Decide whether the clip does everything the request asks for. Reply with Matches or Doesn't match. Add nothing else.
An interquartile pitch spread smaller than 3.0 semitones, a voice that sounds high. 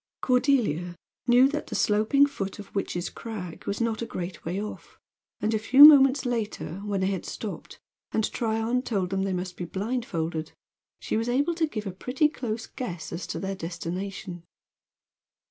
Doesn't match